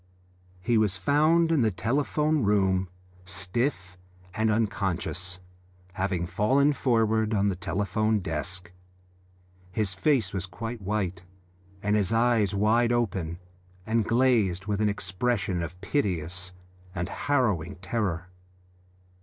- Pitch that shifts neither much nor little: Yes, average, 4.2 semitones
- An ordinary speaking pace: No, slow, 115 wpm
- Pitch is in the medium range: No, low, 105 Hz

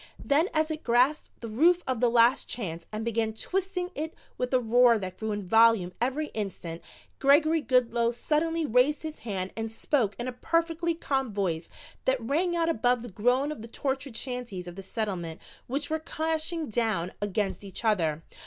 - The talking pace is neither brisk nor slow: Yes, average, 180 wpm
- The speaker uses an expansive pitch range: Yes, wide, 6.1 semitones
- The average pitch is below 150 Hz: No, high, 245 Hz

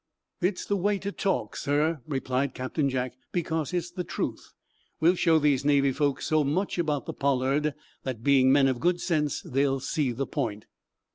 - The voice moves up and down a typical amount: Yes, average, 3.8 semitones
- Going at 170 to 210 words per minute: Yes, average, 180 wpm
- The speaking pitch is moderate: Yes, medium, 145 Hz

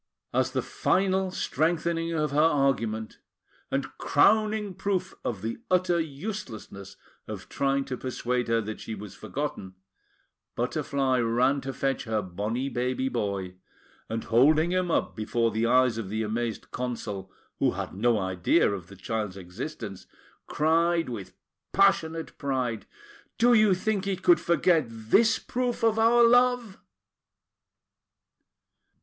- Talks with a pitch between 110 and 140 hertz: Yes, low, 135 Hz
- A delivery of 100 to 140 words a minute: Yes, slow, 135 wpm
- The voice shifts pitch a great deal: Yes, wide, 8.1 semitones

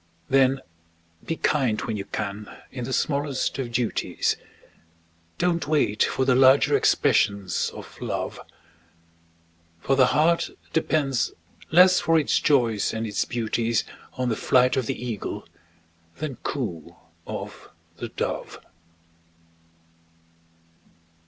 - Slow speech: Yes, slow, 115 wpm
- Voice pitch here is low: Yes, low, 130 Hz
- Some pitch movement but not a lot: Yes, average, 4.3 semitones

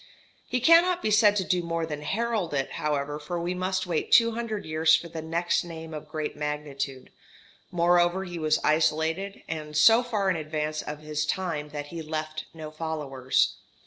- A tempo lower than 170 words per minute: No, average, 180 wpm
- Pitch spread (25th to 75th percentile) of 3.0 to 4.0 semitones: Yes, average, 3.4 semitones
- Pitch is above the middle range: No, medium, 160 Hz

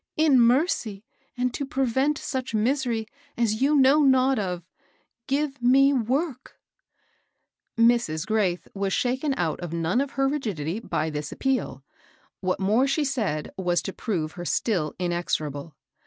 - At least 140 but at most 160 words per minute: Yes, average, 150 wpm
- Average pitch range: No, wide, 7.2 semitones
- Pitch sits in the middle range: No, high, 230 Hz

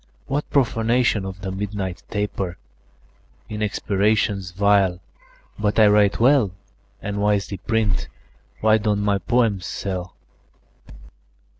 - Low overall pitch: Yes, low, 105 Hz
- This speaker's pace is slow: Yes, slow, 110 wpm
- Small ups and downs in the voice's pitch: Yes, narrow, 2.1 semitones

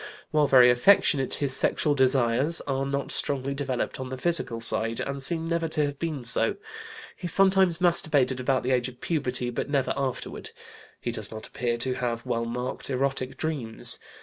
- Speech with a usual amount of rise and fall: Yes, average, 3.2 semitones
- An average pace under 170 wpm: No, average, 175 wpm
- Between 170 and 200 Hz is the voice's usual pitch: No, low, 135 Hz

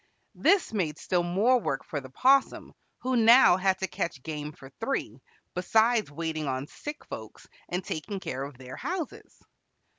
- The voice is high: No, medium, 180 Hz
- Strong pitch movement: Yes, wide, 7.9 semitones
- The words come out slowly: No, average, 160 wpm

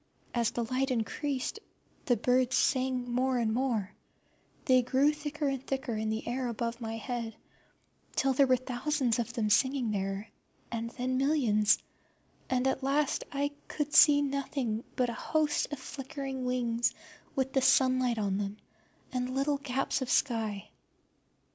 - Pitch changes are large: No, average, 2.7 semitones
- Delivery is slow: No, average, 155 wpm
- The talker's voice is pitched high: Yes, very high, 255 Hz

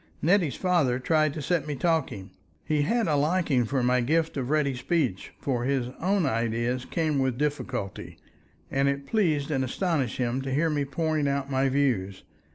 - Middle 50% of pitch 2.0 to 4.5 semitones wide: Yes, average, 3.6 semitones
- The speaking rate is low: No, average, 175 wpm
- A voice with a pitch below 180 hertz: Yes, medium, 140 Hz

